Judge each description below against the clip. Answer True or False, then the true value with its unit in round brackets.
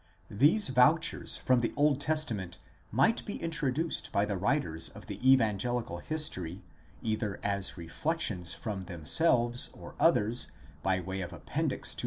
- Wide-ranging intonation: True (7.4 semitones)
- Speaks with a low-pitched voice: True (115 Hz)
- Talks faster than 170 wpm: False (140 wpm)